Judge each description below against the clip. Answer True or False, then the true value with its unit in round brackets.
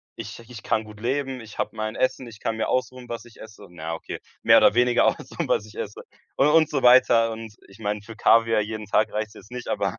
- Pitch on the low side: True (115 Hz)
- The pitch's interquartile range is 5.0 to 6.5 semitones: False (2.6 semitones)